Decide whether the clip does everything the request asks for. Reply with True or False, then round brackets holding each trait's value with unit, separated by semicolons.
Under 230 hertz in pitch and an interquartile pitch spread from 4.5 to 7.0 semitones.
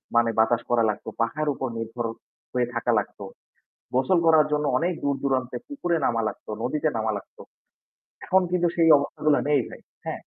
True (135 Hz; 5.0 semitones)